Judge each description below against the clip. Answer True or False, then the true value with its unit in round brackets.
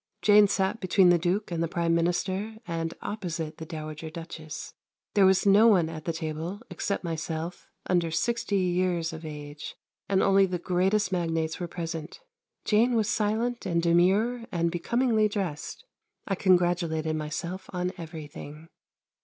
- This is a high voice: False (175 Hz)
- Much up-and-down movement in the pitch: False (3.3 semitones)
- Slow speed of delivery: False (150 wpm)